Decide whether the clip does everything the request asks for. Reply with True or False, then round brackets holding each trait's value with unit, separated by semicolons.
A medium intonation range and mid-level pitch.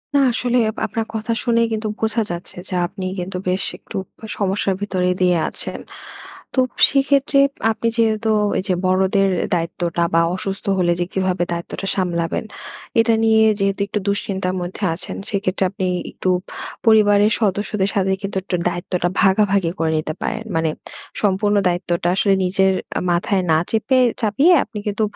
False (3.0 semitones; 195 Hz)